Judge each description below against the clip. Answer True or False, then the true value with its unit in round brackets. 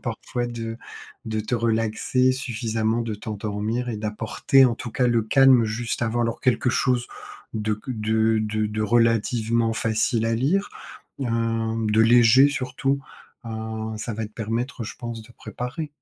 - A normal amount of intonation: False (1.8 semitones)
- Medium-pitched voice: False (115 Hz)